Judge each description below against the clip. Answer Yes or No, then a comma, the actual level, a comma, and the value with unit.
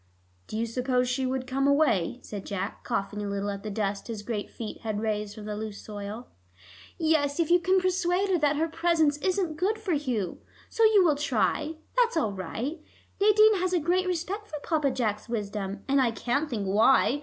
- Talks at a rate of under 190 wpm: No, average, 200 wpm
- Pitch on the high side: Yes, very high, 265 Hz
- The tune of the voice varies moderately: No, wide, 8.2 semitones